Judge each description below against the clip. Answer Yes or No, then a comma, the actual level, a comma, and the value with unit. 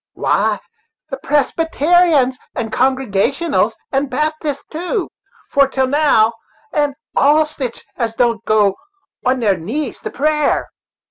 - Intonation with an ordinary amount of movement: Yes, average, 4.1 semitones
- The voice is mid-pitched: No, very high, 275 Hz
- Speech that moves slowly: Yes, slow, 120 wpm